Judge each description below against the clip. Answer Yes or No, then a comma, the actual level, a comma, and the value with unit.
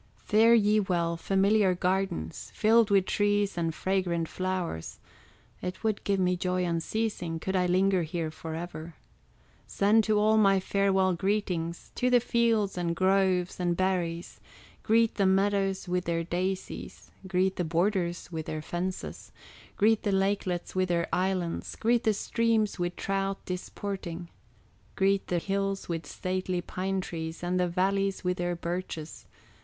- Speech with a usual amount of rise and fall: No, narrow, 2.3 semitones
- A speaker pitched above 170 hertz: Yes, medium, 185 Hz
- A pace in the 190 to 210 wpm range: No, average, 145 wpm